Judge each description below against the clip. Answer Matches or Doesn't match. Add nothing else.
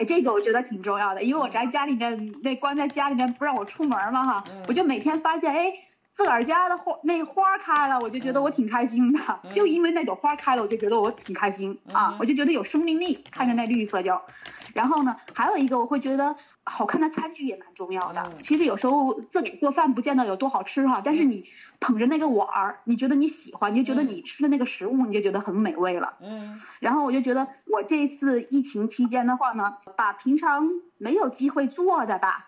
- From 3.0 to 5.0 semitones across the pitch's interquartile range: Matches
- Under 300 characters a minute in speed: Doesn't match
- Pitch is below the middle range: Doesn't match